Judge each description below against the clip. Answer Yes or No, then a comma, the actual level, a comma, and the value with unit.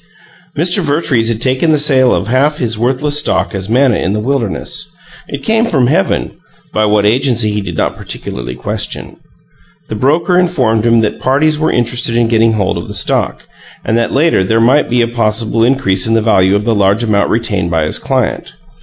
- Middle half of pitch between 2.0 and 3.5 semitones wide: No, average, 4.2 semitones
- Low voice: Yes, low, 115 Hz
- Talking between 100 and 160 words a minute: No, average, 200 wpm